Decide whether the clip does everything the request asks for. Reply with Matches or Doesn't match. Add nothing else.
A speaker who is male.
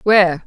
Doesn't match